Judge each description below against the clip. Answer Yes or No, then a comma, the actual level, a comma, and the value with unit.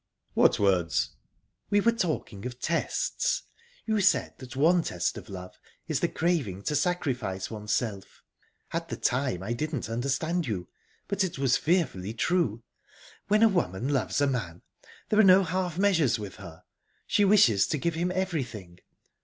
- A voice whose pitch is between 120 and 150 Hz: Yes, medium, 140 Hz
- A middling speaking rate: Yes, average, 160 wpm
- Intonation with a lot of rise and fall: Yes, wide, 9.0 semitones